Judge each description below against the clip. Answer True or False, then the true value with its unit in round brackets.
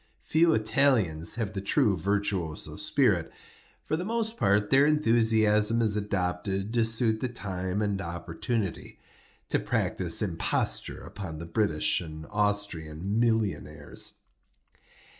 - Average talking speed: False (115 wpm)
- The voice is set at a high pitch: False (105 Hz)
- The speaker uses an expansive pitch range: False (4.0 semitones)